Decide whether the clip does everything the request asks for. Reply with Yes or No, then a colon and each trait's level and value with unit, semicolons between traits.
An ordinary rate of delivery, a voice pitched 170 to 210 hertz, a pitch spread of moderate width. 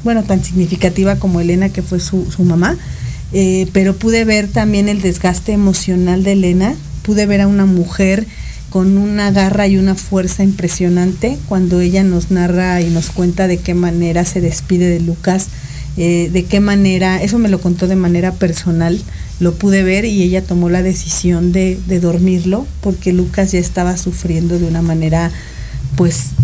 No: average, 175 wpm; medium, 185 Hz; narrow, 1.8 semitones